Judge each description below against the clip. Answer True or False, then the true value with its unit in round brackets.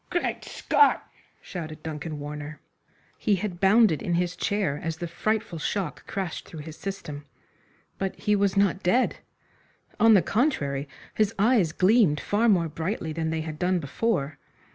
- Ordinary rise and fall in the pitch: True (4.9 semitones)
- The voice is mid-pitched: True (180 Hz)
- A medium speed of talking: True (155 wpm)